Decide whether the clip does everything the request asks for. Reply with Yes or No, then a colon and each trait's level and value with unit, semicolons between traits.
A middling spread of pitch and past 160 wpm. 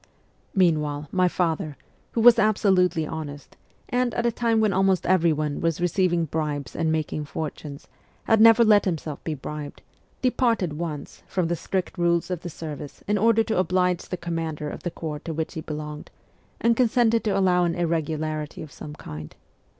Yes: average, 4.1 semitones; average, 175 wpm